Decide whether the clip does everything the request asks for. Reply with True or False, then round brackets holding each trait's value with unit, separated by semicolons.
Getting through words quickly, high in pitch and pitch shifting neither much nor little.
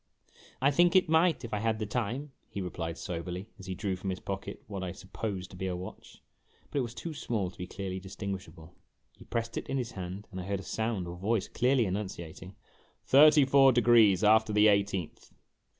False (215 wpm; 100 Hz; 4.2 semitones)